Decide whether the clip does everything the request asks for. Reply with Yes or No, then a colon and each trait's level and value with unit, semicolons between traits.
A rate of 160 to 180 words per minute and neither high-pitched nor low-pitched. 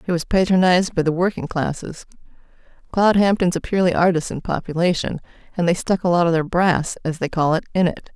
Yes: average, 175 wpm; medium, 175 Hz